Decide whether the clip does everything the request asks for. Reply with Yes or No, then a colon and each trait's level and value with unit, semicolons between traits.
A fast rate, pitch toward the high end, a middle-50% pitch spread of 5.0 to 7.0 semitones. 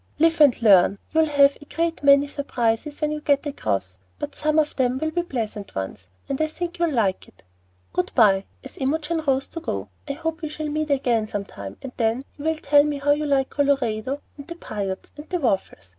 Yes: fast, 215 wpm; very high, 280 Hz; wide, 5.5 semitones